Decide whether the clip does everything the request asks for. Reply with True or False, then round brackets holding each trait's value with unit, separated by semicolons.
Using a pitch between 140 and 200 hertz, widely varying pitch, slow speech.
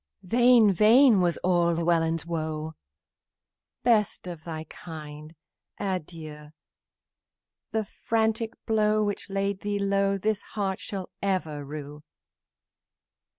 False (190 Hz; 4.7 semitones; 105 wpm)